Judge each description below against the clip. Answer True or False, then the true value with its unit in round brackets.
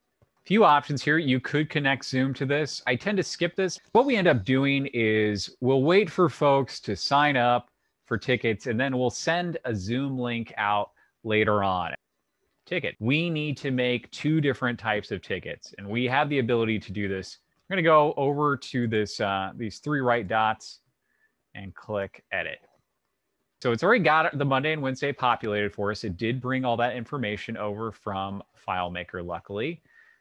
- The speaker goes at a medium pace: True (185 wpm)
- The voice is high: False (125 Hz)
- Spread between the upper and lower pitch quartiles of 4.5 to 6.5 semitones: True (5.2 semitones)